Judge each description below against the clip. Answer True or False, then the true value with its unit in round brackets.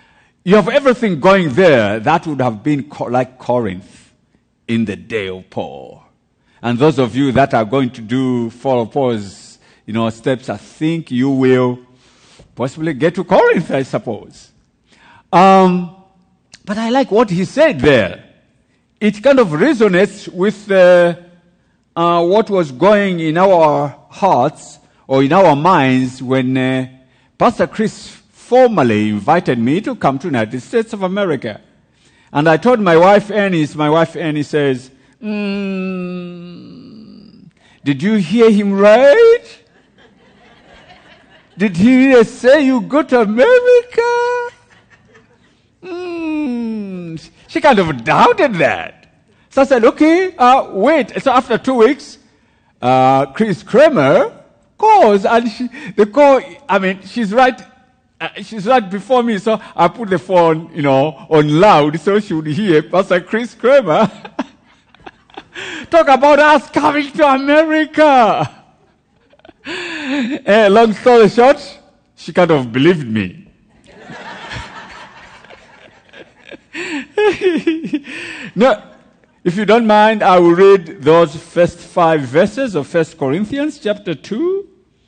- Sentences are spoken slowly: True (130 wpm)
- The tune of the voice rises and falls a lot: True (8.8 semitones)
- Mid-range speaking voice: False (195 Hz)